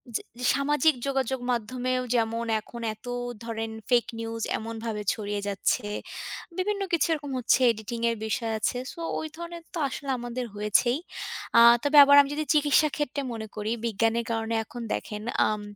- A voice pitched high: Yes, high, 235 Hz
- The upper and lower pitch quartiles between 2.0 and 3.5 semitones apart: No, average, 4.1 semitones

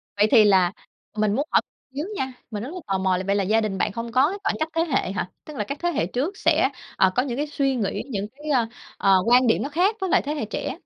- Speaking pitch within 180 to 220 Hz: No, high, 240 Hz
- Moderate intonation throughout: No, wide, 6.3 semitones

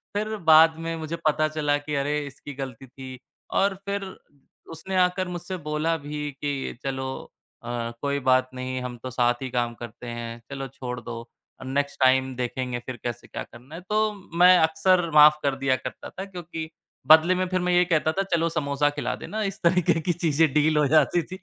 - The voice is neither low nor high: Yes, medium, 150 Hz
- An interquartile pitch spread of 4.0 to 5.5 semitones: Yes, average, 4.7 semitones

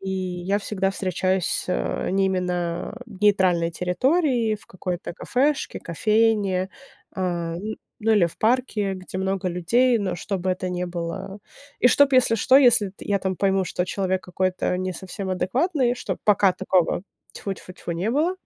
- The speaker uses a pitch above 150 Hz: Yes, high, 190 Hz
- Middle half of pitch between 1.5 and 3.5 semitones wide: Yes, average, 3.2 semitones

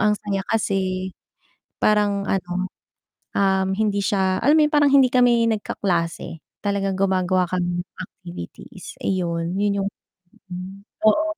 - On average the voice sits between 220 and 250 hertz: No, high, 195 Hz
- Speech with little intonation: Yes, narrow, 2.2 semitones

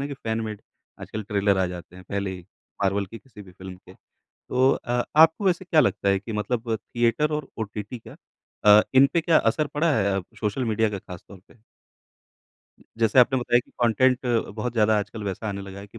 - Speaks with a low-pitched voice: Yes, low, 110 Hz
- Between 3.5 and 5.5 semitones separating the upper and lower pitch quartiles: Yes, average, 4.1 semitones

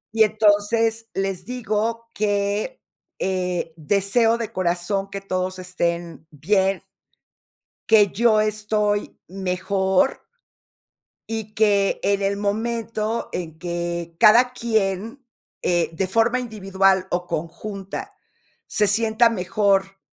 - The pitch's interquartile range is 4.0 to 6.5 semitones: No, average, 2.9 semitones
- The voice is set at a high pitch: Yes, high, 200 Hz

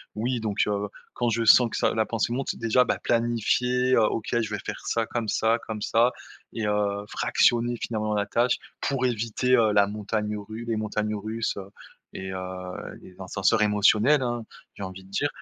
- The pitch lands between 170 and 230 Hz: No, low, 110 Hz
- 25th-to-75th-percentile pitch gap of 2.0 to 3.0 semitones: Yes, narrow, 2.4 semitones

